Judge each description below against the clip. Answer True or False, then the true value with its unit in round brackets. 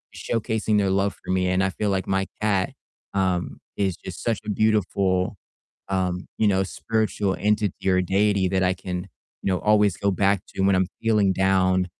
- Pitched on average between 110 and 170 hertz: False (95 Hz)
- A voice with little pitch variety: True (1.9 semitones)